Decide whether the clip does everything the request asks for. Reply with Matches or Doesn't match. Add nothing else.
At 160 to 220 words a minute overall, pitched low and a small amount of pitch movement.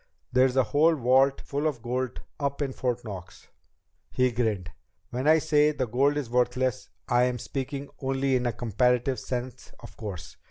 Matches